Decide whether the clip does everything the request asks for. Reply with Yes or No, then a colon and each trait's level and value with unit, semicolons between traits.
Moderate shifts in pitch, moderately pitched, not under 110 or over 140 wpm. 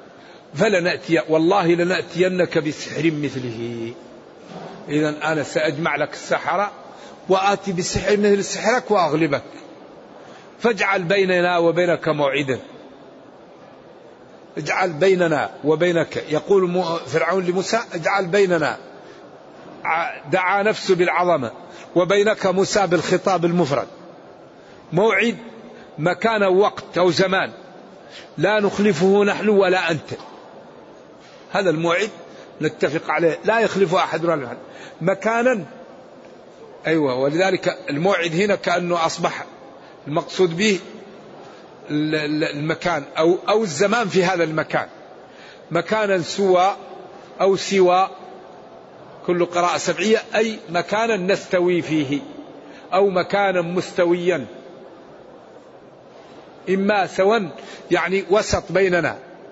No: average, 3.1 semitones; medium, 180 Hz; average, 90 wpm